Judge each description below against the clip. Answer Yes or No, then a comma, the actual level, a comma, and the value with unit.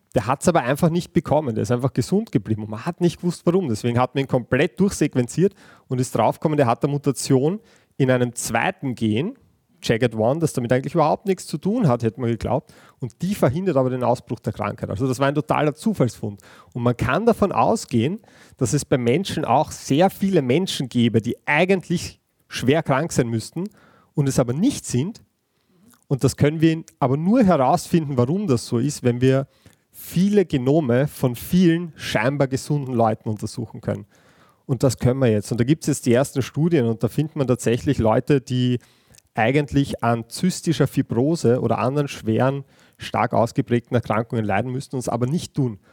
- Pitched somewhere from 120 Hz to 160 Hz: Yes, low, 135 Hz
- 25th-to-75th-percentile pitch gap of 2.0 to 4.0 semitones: No, average, 4.8 semitones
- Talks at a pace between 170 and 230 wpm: Yes, fast, 190 wpm